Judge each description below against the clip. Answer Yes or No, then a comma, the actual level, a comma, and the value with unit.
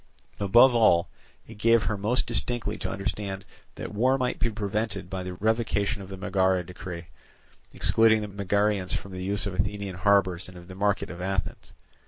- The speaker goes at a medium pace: Yes, average, 180 wpm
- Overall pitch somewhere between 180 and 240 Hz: No, low, 100 Hz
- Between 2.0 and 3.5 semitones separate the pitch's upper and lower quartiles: Yes, narrow, 2.5 semitones